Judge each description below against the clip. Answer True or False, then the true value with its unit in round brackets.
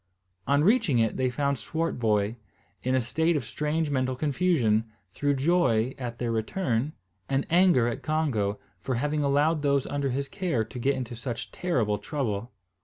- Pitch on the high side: False (135 Hz)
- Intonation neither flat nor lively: True (4.3 semitones)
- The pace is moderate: True (165 wpm)